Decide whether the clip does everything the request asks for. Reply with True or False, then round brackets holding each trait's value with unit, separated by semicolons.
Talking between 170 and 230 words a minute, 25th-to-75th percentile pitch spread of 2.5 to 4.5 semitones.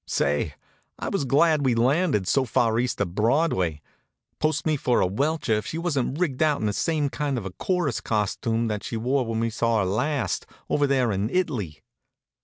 False (200 wpm; 5.5 semitones)